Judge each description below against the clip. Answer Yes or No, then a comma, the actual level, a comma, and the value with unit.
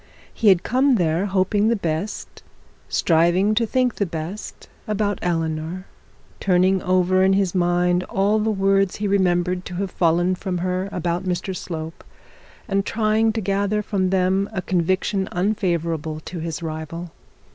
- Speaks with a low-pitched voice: No, medium, 185 Hz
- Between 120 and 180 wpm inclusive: Yes, average, 150 wpm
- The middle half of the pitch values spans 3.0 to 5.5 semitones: No, narrow, 2.4 semitones